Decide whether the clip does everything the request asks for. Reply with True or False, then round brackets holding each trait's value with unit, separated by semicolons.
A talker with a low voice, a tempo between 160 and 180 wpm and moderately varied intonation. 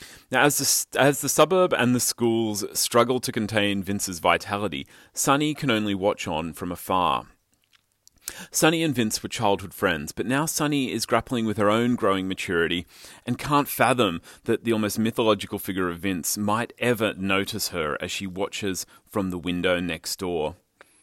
True (105 Hz; 170 wpm; 4.2 semitones)